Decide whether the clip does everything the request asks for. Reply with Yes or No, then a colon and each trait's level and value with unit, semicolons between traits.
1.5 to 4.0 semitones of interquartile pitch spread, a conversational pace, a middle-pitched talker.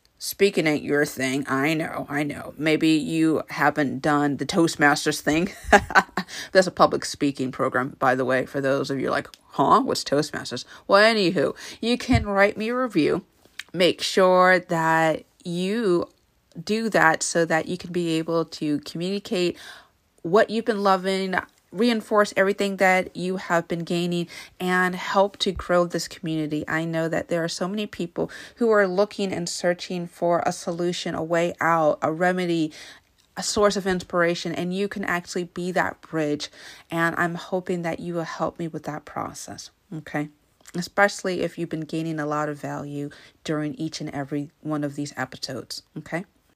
Yes: average, 3.7 semitones; average, 170 wpm; medium, 170 Hz